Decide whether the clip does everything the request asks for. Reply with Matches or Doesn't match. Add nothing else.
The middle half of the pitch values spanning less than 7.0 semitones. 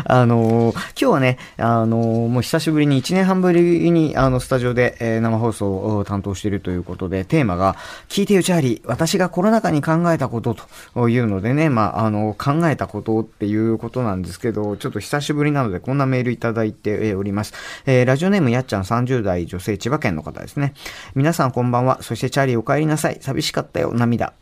Matches